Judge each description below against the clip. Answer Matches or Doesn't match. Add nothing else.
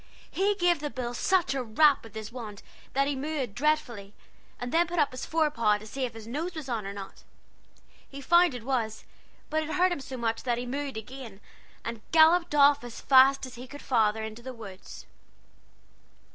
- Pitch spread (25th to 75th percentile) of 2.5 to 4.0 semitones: Doesn't match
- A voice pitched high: Matches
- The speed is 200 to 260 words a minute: Matches